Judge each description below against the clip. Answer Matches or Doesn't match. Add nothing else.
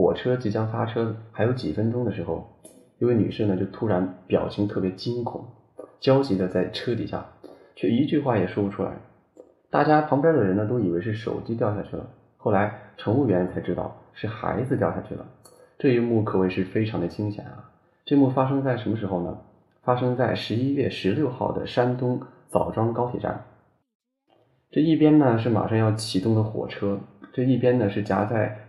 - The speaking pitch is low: Matches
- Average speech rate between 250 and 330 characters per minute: Matches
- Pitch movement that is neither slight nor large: Matches